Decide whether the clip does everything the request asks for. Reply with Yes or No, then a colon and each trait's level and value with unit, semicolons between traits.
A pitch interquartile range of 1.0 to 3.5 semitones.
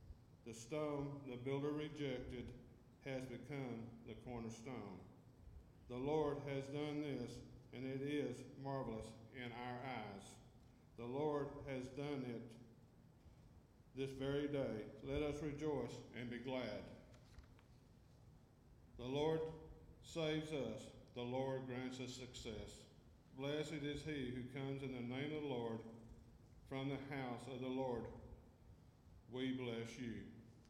Yes: average, 2.7 semitones